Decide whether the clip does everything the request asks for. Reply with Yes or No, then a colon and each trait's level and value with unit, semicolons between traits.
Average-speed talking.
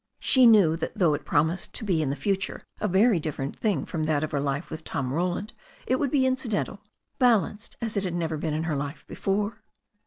No: fast, 220 wpm